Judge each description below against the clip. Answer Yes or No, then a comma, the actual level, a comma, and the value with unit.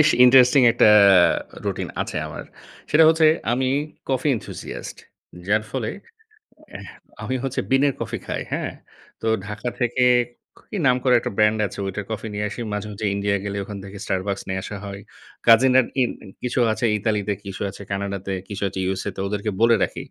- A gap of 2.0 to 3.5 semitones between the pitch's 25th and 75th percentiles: No, average, 3.9 semitones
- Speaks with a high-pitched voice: No, low, 105 Hz